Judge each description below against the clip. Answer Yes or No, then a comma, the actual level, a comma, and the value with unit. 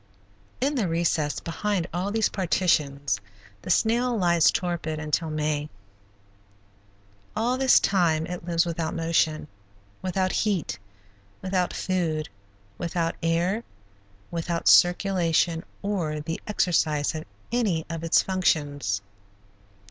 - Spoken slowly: Yes, slow, 110 wpm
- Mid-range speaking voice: Yes, medium, 170 Hz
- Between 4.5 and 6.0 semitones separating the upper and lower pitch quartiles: No, average, 3.0 semitones